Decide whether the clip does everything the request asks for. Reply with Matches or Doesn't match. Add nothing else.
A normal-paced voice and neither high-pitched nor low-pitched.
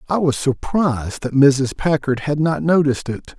Matches